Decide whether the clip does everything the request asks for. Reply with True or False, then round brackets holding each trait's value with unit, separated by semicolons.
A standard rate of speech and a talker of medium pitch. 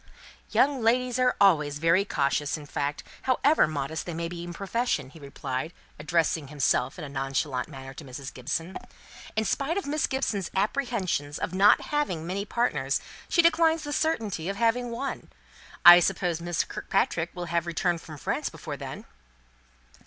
True (165 wpm; 175 Hz)